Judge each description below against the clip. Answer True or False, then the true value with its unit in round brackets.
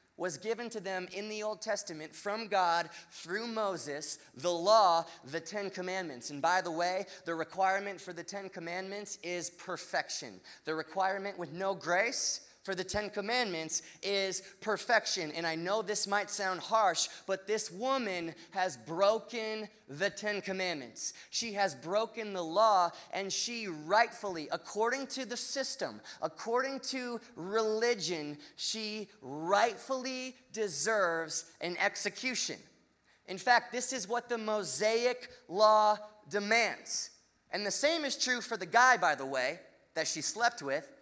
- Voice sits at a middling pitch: False (200 Hz)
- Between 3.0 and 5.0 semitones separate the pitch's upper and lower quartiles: True (4.1 semitones)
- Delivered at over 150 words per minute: False (145 wpm)